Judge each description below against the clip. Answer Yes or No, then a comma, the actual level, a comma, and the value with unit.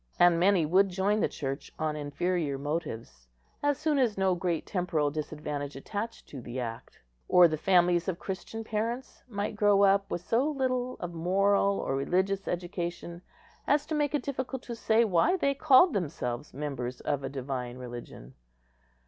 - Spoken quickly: No, average, 165 wpm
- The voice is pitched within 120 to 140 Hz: No, medium, 180 Hz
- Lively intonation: Yes, wide, 6.6 semitones